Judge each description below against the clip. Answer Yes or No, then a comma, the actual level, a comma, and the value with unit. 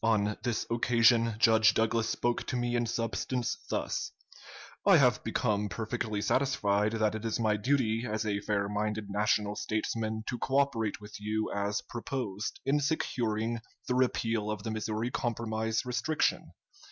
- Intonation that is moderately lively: No, narrow, 1.9 semitones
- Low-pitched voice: Yes, low, 110 Hz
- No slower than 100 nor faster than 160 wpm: Yes, average, 150 wpm